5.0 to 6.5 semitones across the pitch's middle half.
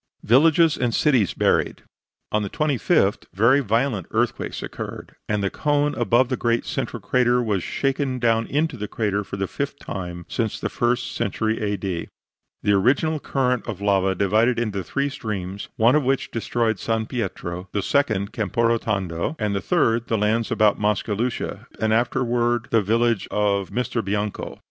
No: average, 3.6 semitones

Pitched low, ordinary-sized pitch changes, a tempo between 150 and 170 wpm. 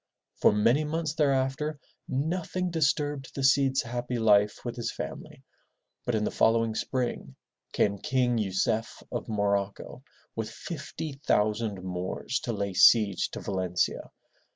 No: low, 120 Hz; average, 4.9 semitones; slow, 135 wpm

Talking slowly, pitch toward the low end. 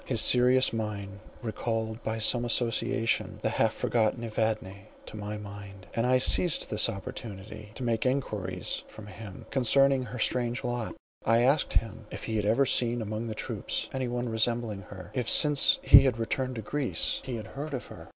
No: average, 180 wpm; low, 115 Hz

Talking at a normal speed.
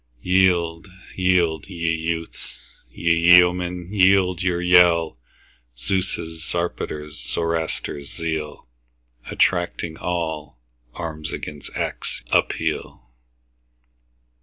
No: slow, 80 wpm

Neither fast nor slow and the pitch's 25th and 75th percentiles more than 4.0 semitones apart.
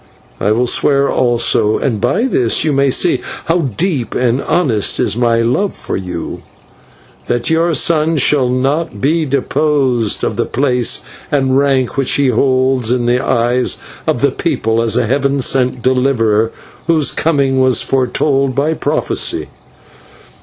No: average, 150 wpm; average, 3.0 semitones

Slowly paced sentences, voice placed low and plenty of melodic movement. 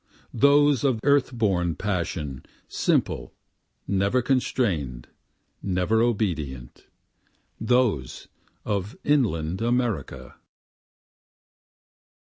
Yes: slow, 70 wpm; low, 105 Hz; wide, 7.0 semitones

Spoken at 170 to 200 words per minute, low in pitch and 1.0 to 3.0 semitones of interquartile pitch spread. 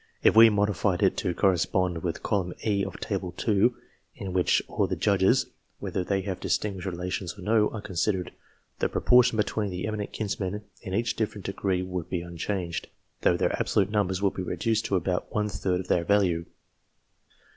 Yes: average, 185 wpm; very low, 95 Hz; narrow, 2.5 semitones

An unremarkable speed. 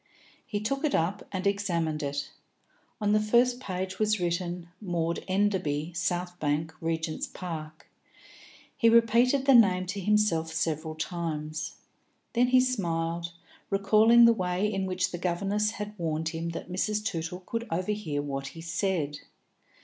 Yes: average, 145 wpm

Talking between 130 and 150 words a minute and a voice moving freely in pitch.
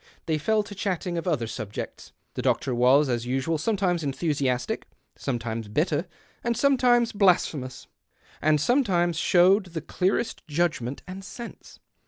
Yes: average, 140 wpm; wide, 6.6 semitones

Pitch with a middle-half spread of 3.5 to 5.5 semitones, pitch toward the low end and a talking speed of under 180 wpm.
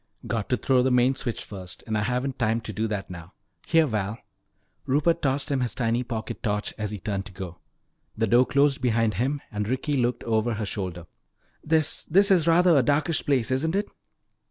No: average, 4.6 semitones; low, 120 Hz; fast, 205 wpm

